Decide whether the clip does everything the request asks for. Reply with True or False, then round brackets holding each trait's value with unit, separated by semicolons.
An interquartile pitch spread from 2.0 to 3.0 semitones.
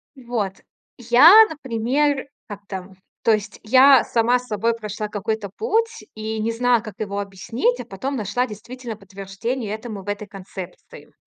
False (3.6 semitones)